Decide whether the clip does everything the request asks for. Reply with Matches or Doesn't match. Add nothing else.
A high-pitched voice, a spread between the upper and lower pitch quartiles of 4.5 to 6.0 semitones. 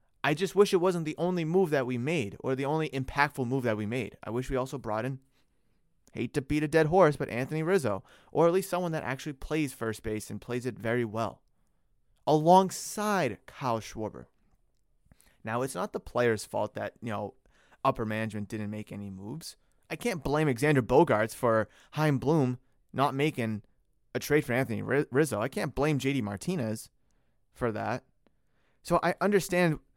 Doesn't match